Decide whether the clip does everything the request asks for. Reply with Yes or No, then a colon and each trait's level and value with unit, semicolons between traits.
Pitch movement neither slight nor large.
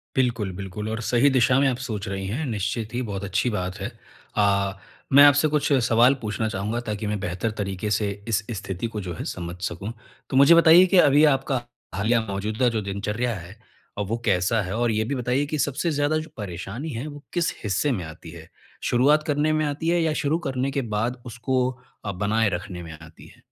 No: wide, 5.7 semitones